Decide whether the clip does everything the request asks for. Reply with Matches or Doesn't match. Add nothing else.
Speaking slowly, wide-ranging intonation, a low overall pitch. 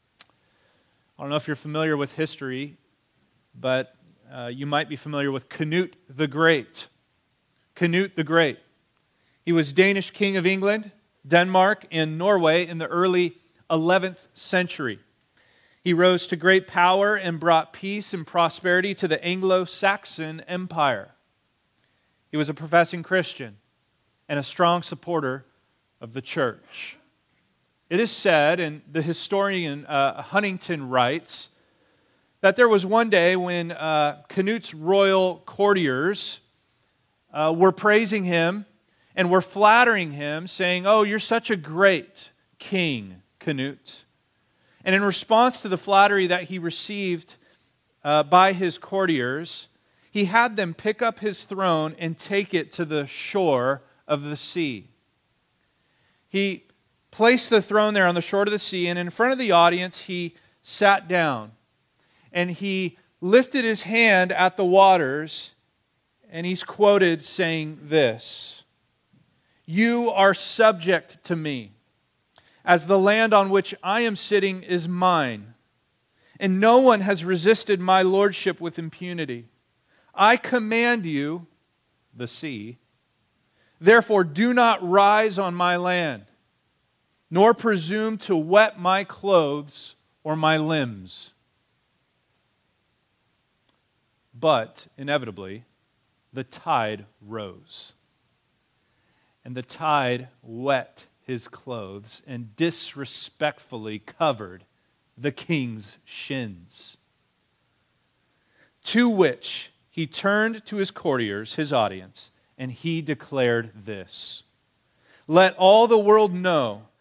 Doesn't match